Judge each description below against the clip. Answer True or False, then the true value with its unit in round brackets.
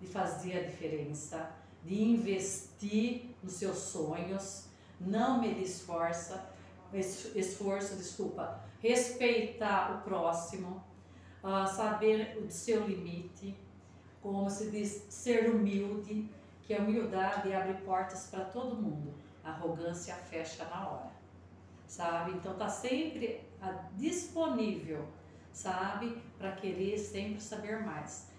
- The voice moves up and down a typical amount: True (4.1 semitones)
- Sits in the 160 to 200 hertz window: True (190 Hz)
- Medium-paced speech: False (110 wpm)